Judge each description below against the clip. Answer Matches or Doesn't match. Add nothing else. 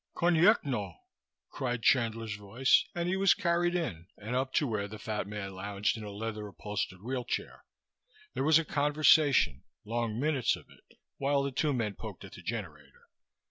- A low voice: Matches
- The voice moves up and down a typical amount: Doesn't match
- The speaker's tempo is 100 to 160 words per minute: Doesn't match